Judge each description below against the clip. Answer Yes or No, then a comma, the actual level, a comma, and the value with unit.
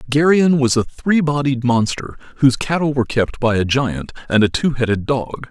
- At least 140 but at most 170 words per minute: No, average, 195 wpm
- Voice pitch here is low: Yes, low, 130 Hz